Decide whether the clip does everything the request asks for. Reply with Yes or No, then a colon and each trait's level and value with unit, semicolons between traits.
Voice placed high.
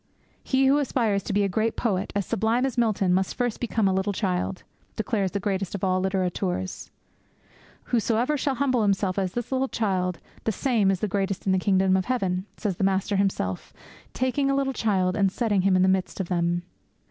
Yes: high, 200 Hz